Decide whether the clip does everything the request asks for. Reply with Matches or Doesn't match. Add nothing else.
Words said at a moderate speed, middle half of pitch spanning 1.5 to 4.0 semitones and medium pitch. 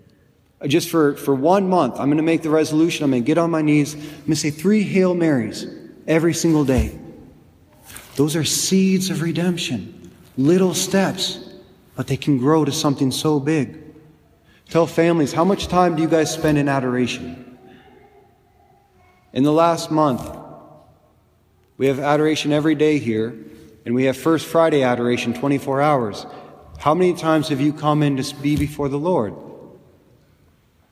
Matches